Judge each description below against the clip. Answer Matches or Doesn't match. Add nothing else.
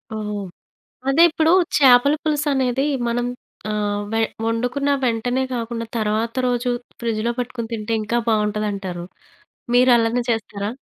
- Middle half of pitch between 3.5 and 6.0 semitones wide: Doesn't match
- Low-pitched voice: Doesn't match